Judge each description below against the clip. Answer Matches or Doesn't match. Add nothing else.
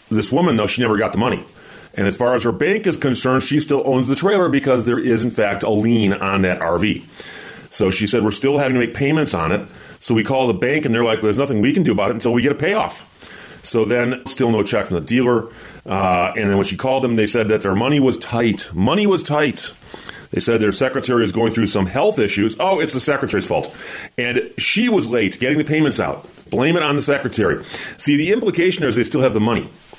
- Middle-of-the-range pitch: Doesn't match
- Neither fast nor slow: Doesn't match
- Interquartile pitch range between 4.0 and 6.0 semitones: Matches